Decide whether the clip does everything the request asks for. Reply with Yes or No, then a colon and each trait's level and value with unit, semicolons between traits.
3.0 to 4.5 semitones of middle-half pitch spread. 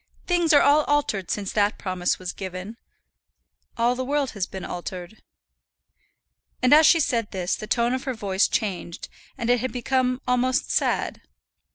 No: average, 5.2 semitones